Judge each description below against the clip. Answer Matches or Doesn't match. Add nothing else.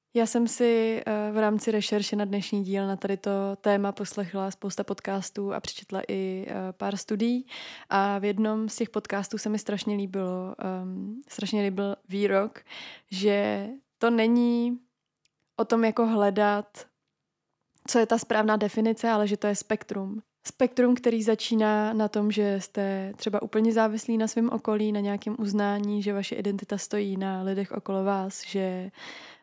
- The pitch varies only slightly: Matches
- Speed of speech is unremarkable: Matches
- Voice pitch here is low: Doesn't match